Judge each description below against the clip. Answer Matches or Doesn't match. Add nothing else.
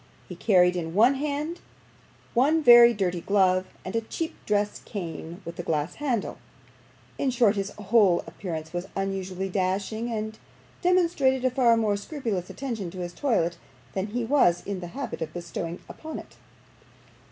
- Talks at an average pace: Matches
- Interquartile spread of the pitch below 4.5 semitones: Doesn't match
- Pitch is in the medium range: Doesn't match